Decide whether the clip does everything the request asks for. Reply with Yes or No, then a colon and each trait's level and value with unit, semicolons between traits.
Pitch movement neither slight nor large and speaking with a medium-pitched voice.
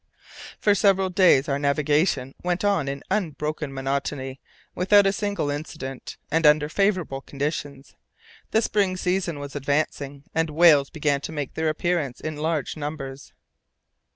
Yes: average, 4.2 semitones; medium, 150 Hz